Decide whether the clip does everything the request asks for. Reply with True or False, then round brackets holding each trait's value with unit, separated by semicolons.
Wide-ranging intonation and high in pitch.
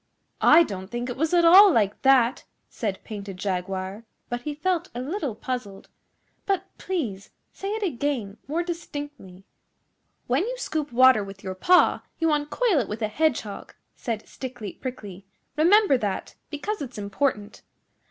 True (7.7 semitones; 255 Hz)